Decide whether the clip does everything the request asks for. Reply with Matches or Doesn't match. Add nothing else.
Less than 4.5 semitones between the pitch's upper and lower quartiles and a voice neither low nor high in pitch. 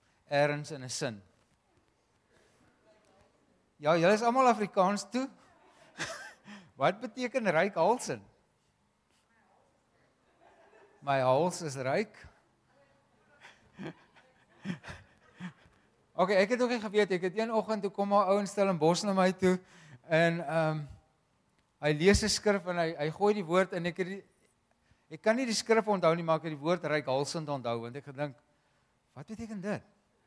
Doesn't match